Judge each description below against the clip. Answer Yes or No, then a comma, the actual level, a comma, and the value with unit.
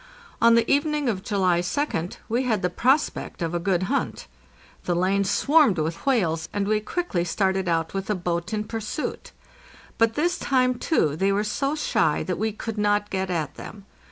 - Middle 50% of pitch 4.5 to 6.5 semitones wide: Yes, average, 4.8 semitones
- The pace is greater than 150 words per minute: Yes, average, 185 wpm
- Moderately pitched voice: No, high, 205 Hz